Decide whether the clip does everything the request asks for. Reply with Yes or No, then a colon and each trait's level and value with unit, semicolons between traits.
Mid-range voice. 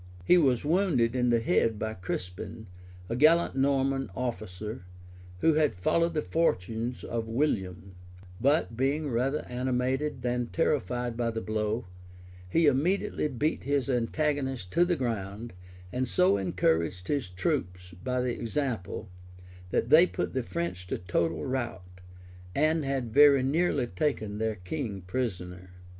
No: low, 125 Hz